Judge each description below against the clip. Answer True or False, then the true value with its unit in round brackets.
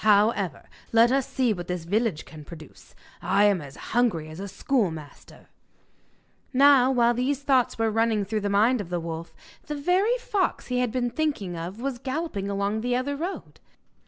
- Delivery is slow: False (180 wpm)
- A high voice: True (225 Hz)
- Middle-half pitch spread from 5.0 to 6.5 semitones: True (5.3 semitones)